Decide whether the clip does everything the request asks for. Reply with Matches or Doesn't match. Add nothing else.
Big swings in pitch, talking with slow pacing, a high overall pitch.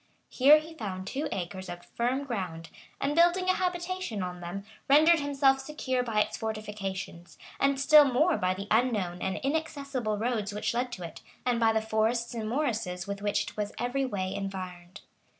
Doesn't match